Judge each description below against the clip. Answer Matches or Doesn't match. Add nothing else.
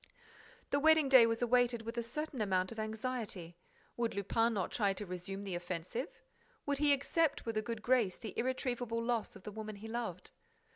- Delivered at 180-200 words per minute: Matches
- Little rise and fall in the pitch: Doesn't match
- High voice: Matches